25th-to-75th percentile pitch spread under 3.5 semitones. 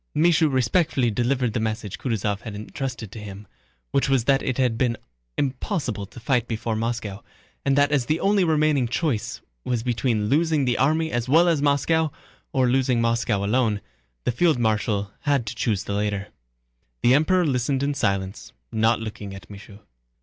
No: average, 4.6 semitones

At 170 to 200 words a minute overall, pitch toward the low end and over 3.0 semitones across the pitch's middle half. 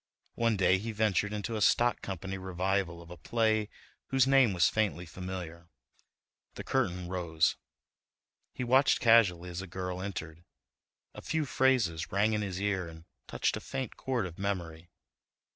No: average, 155 wpm; very low, 95 Hz; average, 4.0 semitones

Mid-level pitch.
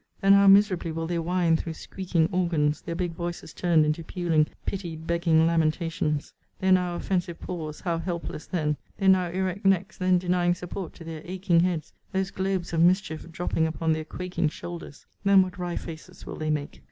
Yes: medium, 175 Hz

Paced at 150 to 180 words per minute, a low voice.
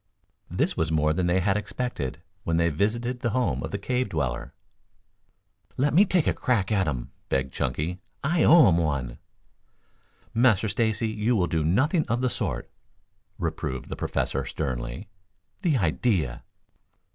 Yes: average, 155 wpm; low, 100 Hz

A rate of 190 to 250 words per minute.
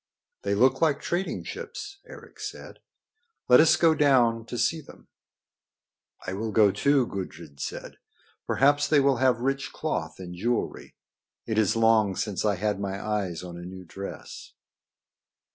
No: average, 155 wpm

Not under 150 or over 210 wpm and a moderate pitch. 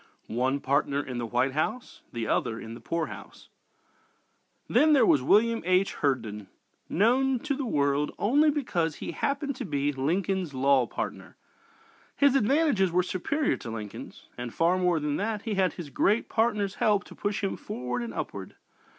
Yes: average, 170 wpm; medium, 175 Hz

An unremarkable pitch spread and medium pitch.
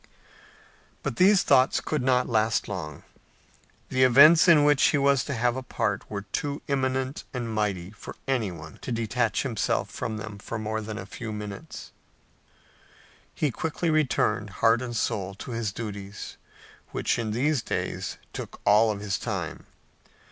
No: average, 4.2 semitones; low, 115 Hz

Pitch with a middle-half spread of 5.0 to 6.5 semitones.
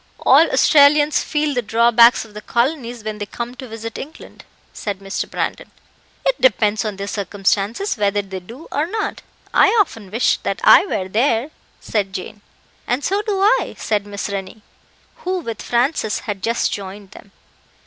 Yes: wide, 5.6 semitones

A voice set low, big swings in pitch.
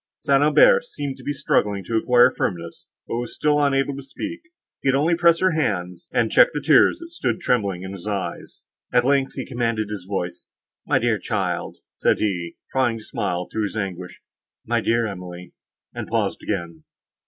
Yes: low, 115 Hz; wide, 6.8 semitones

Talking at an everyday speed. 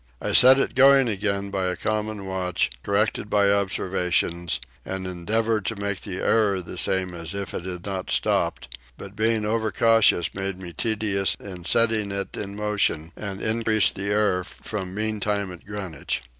Yes: average, 170 wpm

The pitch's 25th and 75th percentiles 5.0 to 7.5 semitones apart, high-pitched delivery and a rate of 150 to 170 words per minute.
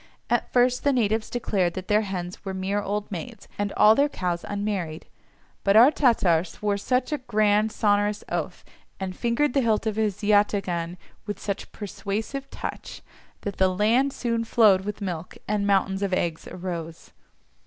No: average, 2.9 semitones; high, 205 Hz; average, 165 wpm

